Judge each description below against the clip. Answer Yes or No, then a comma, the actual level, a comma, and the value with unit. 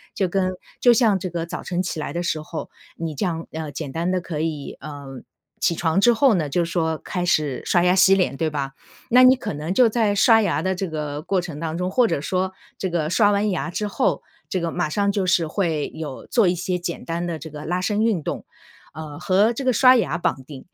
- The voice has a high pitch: No, medium, 175 Hz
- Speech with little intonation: No, average, 3.8 semitones